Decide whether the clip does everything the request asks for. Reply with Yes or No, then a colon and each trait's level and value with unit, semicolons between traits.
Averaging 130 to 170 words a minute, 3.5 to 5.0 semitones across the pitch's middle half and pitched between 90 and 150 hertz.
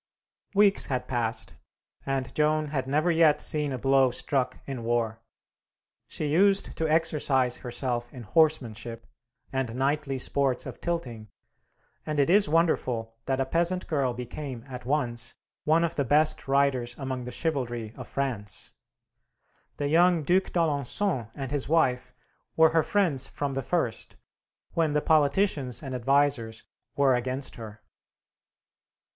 Yes: average, 140 wpm; average, 4.0 semitones; low, 135 Hz